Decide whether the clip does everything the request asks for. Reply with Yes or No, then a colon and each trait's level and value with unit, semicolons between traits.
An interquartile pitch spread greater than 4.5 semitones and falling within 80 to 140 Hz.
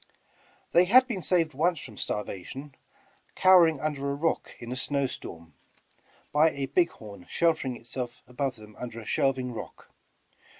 Yes: average, 5.3 semitones; low, 135 Hz